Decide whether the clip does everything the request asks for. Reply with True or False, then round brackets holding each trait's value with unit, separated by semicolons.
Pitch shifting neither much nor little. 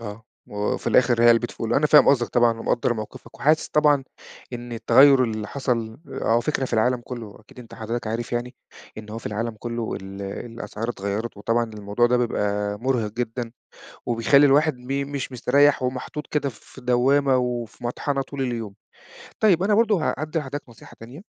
True (3.2 semitones)